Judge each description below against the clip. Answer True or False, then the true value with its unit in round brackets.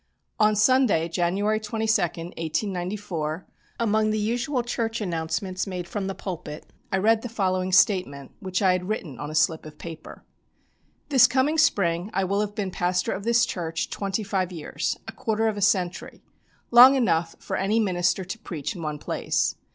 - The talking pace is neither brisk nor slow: True (175 wpm)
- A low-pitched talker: False (190 Hz)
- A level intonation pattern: False (3.9 semitones)